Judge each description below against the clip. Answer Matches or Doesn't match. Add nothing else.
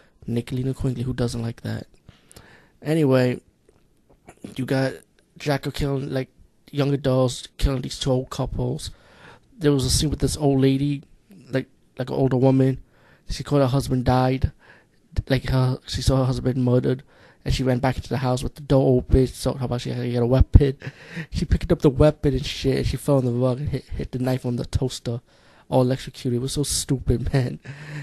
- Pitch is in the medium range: Doesn't match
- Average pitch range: Doesn't match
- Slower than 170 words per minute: Doesn't match